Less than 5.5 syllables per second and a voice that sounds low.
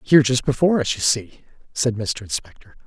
No: 5.9 syllables/s; low, 125 Hz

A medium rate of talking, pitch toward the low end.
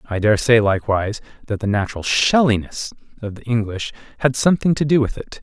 Yes: average, 175 wpm; low, 115 Hz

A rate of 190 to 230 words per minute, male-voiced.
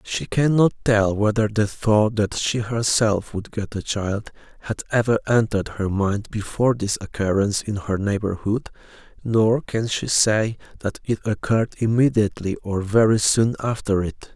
No: average, 155 wpm; male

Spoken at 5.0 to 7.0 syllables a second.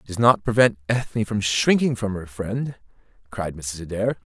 No: 4.7 syllables/s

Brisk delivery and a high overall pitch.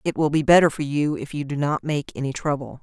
No: fast, 275 wpm; medium, 145 Hz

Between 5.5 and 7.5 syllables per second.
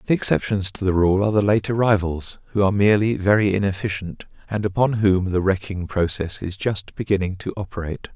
Yes: 6.0 syllables/s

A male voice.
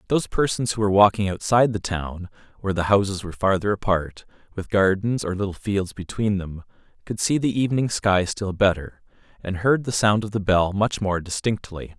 Yes: male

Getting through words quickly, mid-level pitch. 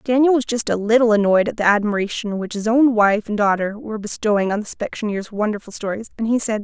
No: fast, 225 wpm; high, 215 Hz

